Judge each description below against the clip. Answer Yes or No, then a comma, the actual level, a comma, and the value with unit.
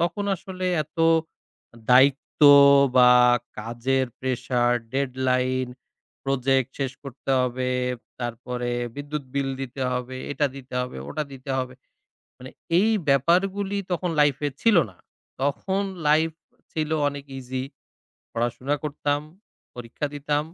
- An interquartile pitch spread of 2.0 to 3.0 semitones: Yes, average, 2.7 semitones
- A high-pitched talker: No, low, 135 Hz